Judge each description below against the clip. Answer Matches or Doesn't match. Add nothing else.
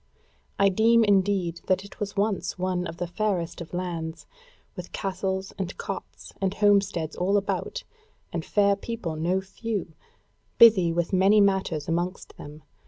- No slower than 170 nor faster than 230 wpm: Doesn't match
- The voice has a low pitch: Doesn't match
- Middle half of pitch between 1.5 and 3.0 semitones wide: Matches